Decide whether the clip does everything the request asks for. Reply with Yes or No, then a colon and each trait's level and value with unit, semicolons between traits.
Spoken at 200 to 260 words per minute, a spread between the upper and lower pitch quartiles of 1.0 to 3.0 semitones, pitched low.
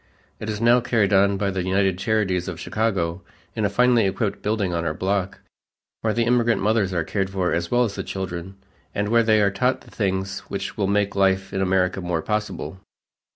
Yes: fast, 205 wpm; narrow, 2.4 semitones; low, 100 Hz